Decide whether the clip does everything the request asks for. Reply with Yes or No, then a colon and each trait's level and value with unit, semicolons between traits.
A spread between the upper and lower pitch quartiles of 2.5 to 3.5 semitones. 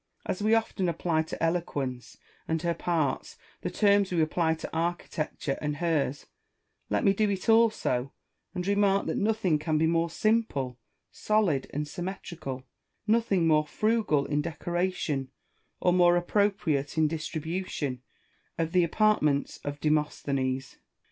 No: average, 4.6 semitones